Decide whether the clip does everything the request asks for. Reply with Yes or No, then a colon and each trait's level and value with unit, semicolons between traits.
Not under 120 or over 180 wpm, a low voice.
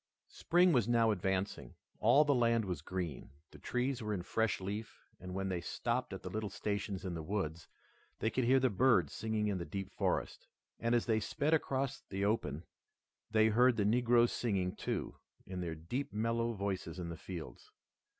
No: average, 190 wpm; low, 105 Hz